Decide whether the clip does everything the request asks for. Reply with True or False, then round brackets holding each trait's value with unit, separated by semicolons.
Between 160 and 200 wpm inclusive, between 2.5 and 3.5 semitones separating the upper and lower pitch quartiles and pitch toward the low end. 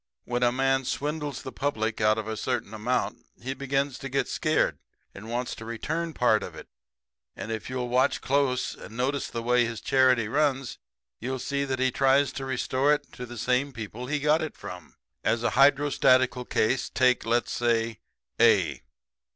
True (185 wpm; 2.8 semitones; 130 Hz)